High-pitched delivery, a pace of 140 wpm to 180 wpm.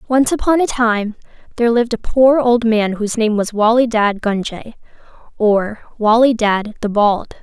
Yes: high, 225 Hz; average, 170 wpm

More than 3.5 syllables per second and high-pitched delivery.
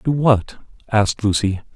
No: 4.7 syllables/s; low, 110 Hz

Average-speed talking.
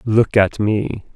Yes: average, 155 wpm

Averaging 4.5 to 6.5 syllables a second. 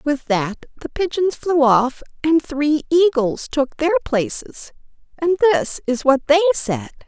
No: 3.9 syllables/s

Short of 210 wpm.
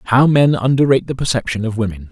Yes: average, 200 wpm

